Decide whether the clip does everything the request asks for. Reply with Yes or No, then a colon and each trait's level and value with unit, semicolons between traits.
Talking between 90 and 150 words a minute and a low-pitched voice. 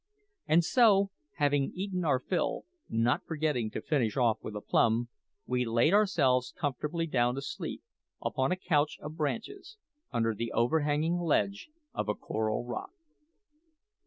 No: average, 145 wpm; medium, 145 Hz